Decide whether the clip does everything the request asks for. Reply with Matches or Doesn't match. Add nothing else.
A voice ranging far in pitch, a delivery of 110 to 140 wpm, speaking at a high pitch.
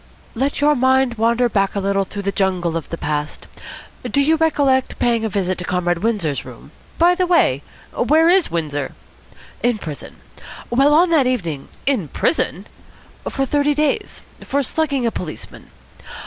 Doesn't match